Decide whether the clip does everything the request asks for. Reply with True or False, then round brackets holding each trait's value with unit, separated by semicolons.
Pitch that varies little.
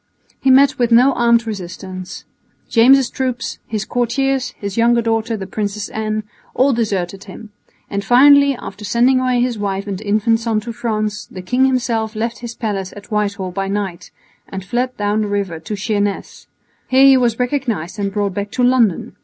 False (3.4 semitones)